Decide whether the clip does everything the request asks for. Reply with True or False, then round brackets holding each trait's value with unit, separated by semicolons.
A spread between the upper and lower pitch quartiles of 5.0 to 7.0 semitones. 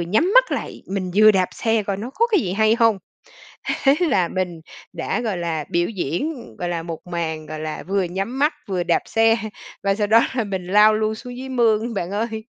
False (4.5 semitones)